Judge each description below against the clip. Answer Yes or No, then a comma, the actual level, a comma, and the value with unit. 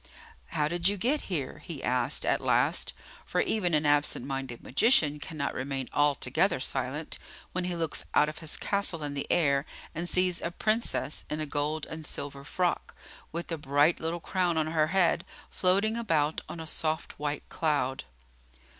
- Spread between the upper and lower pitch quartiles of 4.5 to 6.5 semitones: No, average, 3.2 semitones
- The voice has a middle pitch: Yes, medium, 155 Hz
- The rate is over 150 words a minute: Yes, average, 170 wpm